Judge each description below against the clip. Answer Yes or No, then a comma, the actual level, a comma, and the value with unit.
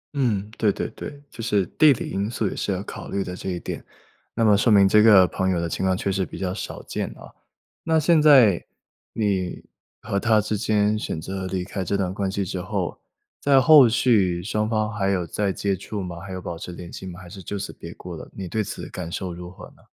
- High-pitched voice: No, low, 100 Hz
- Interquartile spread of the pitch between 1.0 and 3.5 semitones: Yes, average, 2.7 semitones